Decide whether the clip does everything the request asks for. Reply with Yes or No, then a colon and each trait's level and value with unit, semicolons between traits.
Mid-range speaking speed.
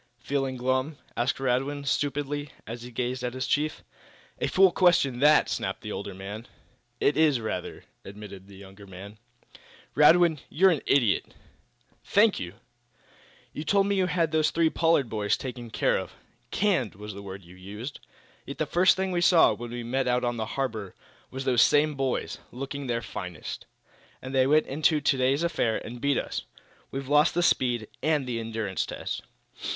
Yes: average, 175 wpm